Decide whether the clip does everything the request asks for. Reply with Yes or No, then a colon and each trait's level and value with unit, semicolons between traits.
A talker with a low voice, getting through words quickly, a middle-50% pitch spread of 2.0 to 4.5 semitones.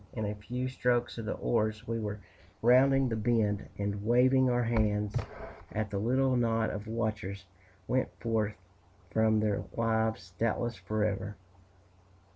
No: low, 110 Hz; average, 140 wpm; narrow, 2.4 semitones